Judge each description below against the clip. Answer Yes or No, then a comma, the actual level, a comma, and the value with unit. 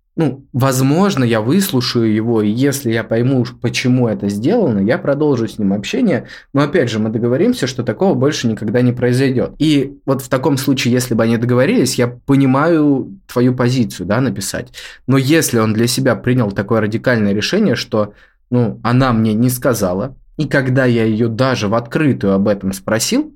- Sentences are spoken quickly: Yes, fast, 175 wpm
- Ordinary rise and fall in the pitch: Yes, average, 3.2 semitones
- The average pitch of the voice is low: Yes, low, 125 Hz